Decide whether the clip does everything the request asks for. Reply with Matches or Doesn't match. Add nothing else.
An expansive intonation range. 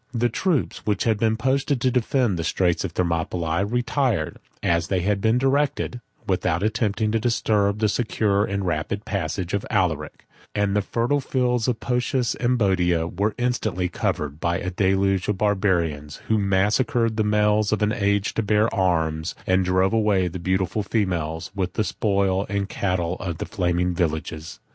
Doesn't match